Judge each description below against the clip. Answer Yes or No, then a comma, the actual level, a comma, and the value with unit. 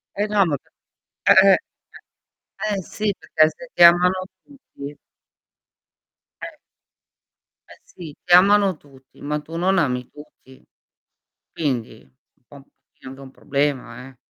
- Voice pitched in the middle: Yes, medium, 155 Hz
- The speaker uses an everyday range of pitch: No, wide, 5.7 semitones